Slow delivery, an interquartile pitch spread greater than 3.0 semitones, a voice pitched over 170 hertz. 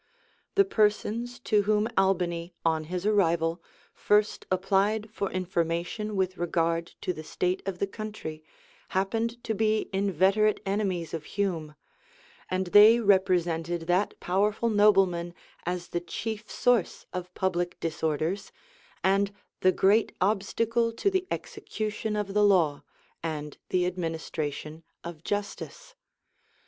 Yes: slow, 125 wpm; average, 3.6 semitones; high, 190 Hz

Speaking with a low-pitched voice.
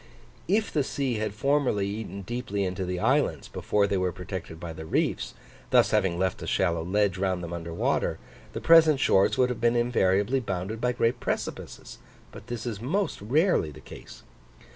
Yes: low, 100 Hz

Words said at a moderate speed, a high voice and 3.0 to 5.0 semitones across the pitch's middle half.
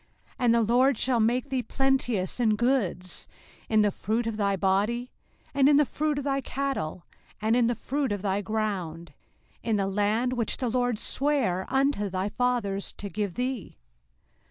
Yes: average, 180 wpm; high, 230 Hz; average, 4.2 semitones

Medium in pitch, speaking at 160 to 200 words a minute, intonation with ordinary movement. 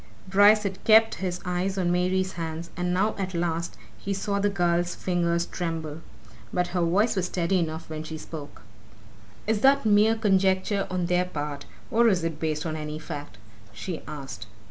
Yes: medium, 180 Hz; average, 175 wpm; average, 3.0 semitones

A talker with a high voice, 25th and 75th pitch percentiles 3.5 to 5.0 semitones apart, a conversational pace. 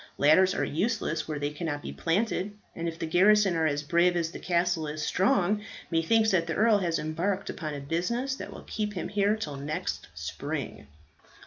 No: medium, 170 Hz; average, 4.5 semitones; average, 195 wpm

